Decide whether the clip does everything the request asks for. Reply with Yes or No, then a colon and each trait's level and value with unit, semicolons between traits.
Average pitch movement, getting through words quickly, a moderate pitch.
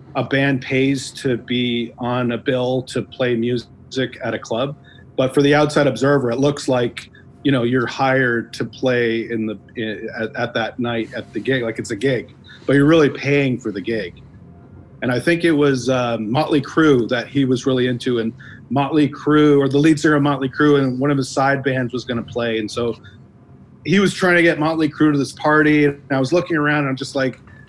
No: average, 3.0 semitones; fast, 225 wpm; low, 130 Hz